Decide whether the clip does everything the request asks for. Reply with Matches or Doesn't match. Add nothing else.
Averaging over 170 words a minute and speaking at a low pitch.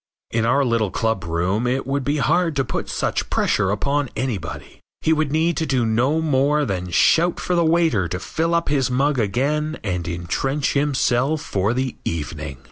Matches